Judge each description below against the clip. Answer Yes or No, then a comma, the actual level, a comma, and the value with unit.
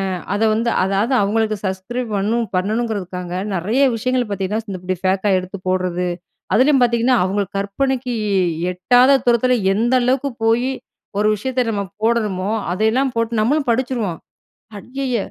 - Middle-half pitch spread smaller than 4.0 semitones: No, average, 4.3 semitones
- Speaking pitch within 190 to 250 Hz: Yes, high, 225 Hz